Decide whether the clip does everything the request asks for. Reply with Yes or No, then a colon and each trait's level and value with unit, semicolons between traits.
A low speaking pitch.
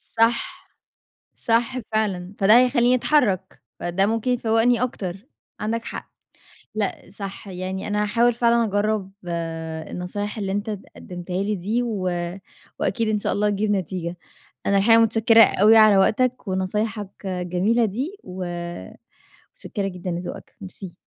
No: high, 210 Hz